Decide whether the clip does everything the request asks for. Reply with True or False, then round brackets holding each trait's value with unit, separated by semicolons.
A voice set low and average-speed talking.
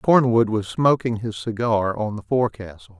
True (110 Hz; 160 wpm)